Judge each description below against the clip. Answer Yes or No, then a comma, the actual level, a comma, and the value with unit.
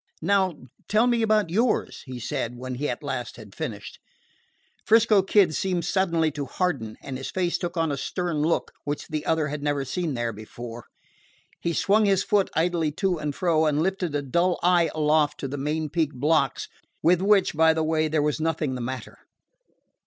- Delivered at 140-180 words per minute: No, average, 190 wpm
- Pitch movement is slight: No, average, 4.1 semitones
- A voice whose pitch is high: No, medium, 160 Hz